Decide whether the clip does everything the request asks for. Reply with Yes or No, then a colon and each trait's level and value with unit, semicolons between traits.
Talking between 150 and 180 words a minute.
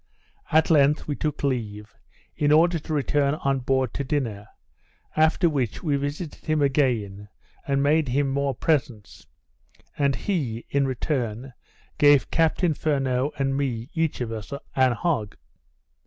No: average, 140 wpm